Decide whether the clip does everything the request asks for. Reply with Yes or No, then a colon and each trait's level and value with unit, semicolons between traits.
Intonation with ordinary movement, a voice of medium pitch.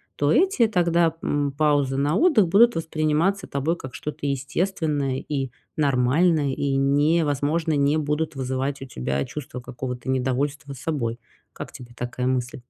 Yes: average, 3.5 semitones; medium, 145 Hz